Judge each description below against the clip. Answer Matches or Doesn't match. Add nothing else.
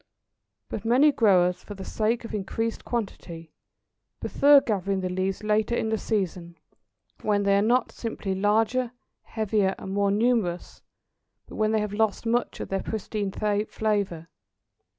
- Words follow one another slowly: Doesn't match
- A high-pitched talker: Matches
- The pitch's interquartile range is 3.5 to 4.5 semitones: Doesn't match